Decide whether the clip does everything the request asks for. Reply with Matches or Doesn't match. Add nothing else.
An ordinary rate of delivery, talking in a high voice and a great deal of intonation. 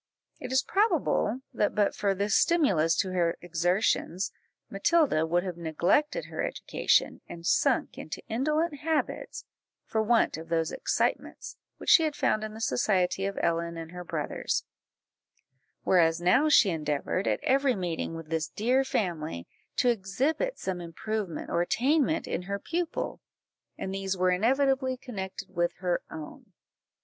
Matches